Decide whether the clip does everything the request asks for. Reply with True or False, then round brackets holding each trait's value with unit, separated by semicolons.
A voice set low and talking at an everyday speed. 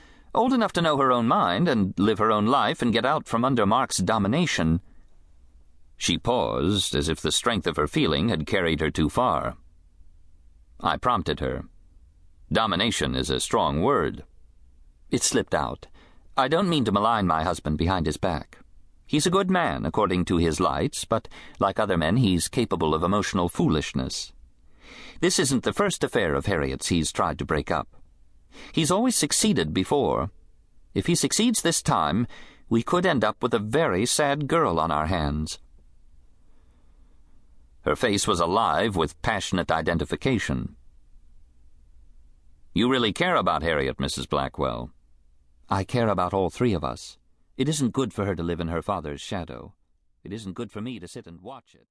True (80 Hz; 170 wpm)